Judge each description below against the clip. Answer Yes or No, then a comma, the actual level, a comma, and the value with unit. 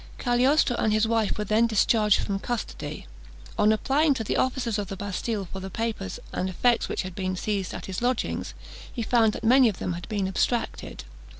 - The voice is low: No, high, 215 Hz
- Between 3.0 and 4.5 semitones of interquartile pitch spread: Yes, average, 3.6 semitones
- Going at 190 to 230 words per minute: Yes, average, 200 wpm